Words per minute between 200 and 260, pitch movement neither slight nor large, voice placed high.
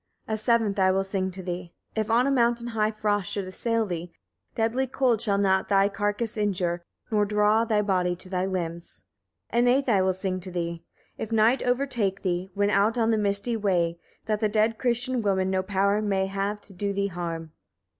Yes: fast, 205 wpm; average, 3.0 semitones; high, 200 Hz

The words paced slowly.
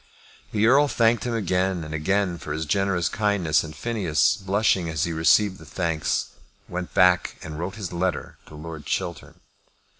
No: average, 170 wpm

